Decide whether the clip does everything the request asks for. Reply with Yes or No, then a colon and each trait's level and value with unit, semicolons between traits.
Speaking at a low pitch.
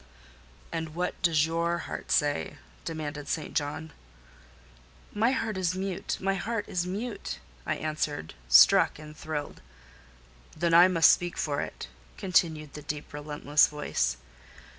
No: medium, 160 Hz